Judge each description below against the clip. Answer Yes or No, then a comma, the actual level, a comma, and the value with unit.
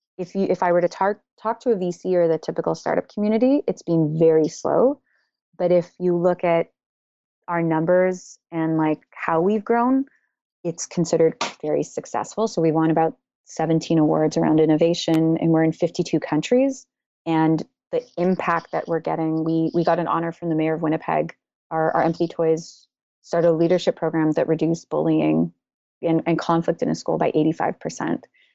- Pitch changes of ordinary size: No, narrow, 2.0 semitones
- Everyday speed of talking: Yes, average, 175 wpm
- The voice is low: No, medium, 165 Hz